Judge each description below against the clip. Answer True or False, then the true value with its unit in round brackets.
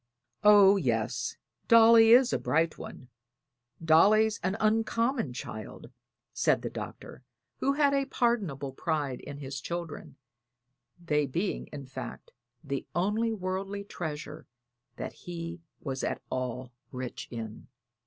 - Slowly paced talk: True (125 wpm)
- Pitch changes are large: True (7.8 semitones)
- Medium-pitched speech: True (170 Hz)